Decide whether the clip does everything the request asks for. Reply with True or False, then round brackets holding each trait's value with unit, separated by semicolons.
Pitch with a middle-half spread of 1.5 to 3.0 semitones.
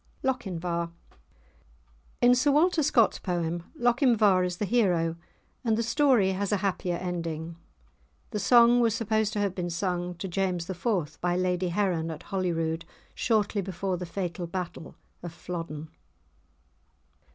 False (4.1 semitones)